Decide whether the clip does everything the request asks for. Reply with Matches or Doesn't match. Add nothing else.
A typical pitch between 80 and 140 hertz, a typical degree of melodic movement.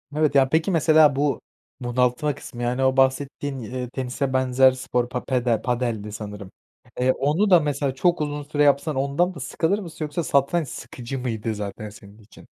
Matches